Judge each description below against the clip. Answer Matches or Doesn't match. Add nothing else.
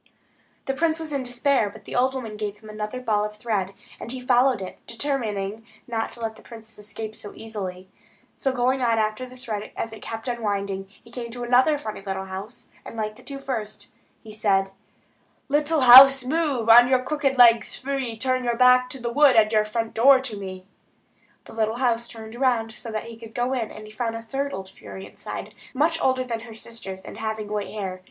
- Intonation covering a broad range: Doesn't match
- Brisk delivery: Matches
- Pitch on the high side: Matches